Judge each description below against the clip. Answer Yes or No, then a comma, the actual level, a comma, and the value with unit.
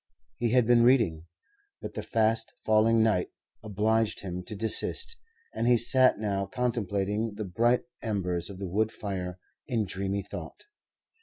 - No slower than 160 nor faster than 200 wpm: No, average, 150 wpm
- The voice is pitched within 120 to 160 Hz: No, low, 110 Hz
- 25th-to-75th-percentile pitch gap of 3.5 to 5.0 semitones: No, average, 2.9 semitones